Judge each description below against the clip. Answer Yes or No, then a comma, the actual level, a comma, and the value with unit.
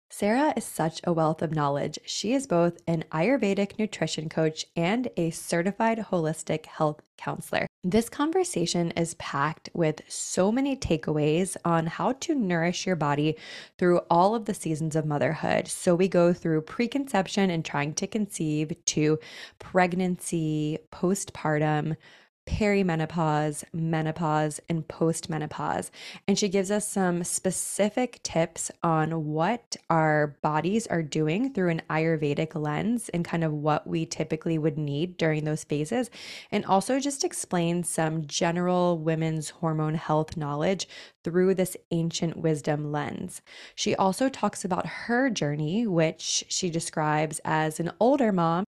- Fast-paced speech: No, average, 140 wpm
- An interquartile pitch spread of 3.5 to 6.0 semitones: Yes, average, 3.9 semitones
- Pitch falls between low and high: Yes, medium, 170 Hz